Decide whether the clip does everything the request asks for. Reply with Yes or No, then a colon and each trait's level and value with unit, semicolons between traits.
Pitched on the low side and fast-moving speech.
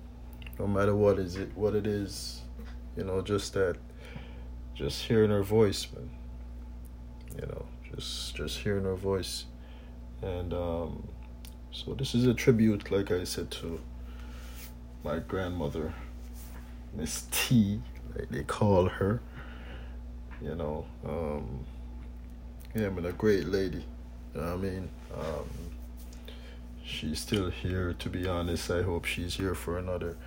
No: very low, 75 Hz; average, 140 wpm